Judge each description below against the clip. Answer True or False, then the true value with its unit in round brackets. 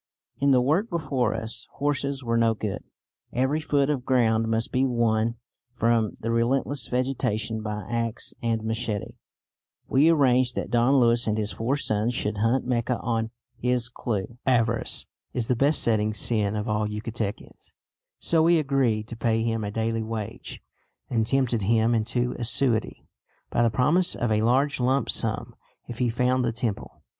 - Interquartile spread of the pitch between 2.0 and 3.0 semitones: True (2.6 semitones)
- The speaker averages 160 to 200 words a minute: True (165 wpm)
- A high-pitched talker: False (115 Hz)